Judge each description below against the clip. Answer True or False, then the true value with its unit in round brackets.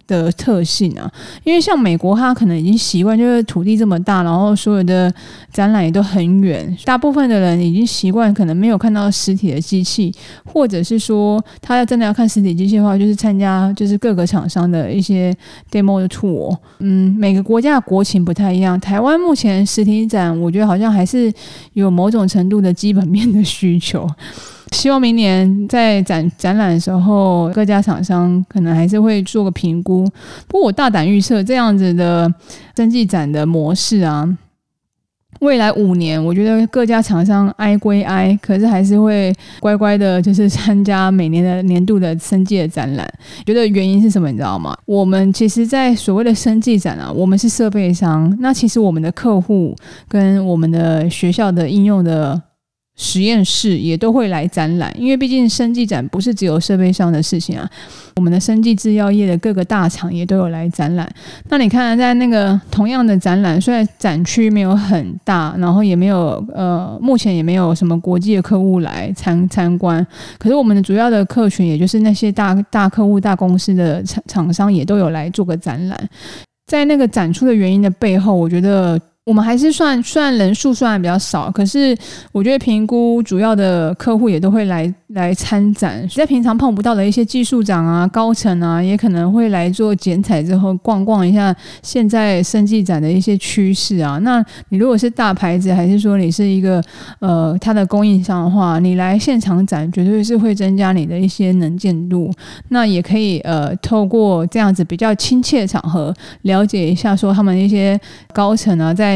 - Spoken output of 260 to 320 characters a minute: True (290 characters per minute)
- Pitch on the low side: False (195 Hz)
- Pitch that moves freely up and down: False (3.2 semitones)